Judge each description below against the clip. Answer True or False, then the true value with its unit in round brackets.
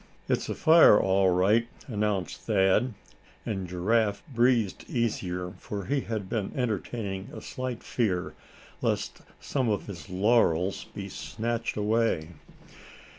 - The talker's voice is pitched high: False (105 Hz)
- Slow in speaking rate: True (125 wpm)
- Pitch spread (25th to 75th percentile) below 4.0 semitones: True (3.6 semitones)